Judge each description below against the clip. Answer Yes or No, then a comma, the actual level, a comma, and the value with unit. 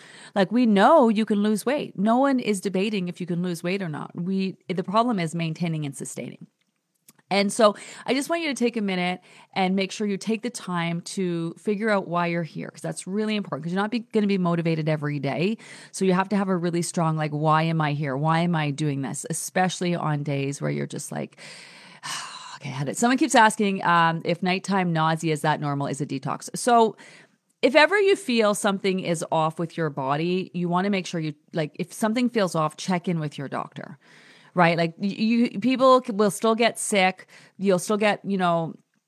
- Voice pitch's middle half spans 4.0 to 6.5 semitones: Yes, average, 4.3 semitones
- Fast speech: Yes, fast, 225 wpm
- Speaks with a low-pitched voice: No, medium, 185 Hz